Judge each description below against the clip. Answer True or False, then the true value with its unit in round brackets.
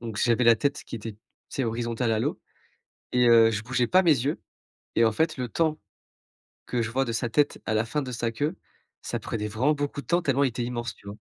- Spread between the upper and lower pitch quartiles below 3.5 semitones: False (3.8 semitones)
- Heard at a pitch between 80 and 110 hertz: False (120 Hz)